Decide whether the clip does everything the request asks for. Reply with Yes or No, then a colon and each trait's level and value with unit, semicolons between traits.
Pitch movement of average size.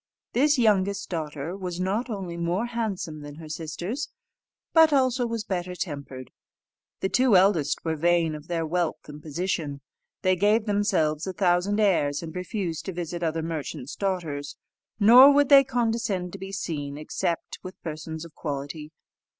Yes: average, 4.6 semitones